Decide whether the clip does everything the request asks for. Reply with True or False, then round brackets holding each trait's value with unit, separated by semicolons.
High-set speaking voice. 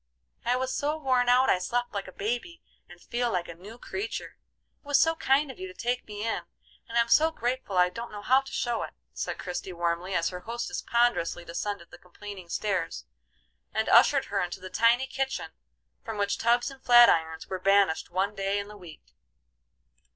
True (220 Hz)